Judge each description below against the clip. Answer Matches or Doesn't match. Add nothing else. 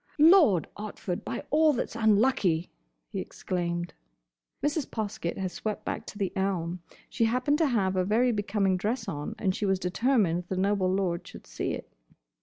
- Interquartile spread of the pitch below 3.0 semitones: Doesn't match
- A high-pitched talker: Matches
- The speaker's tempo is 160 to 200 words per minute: Matches